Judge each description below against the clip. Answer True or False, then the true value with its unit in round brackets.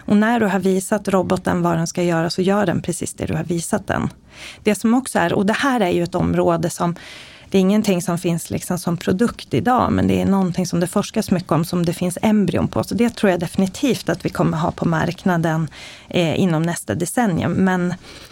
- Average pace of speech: False (230 wpm)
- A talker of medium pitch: True (180 Hz)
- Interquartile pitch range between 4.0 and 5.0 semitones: False (3.1 semitones)